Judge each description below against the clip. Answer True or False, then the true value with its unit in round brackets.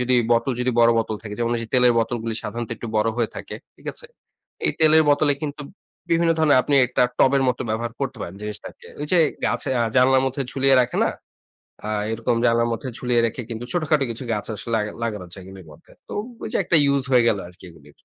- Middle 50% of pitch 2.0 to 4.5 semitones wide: True (3.5 semitones)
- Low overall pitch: True (120 Hz)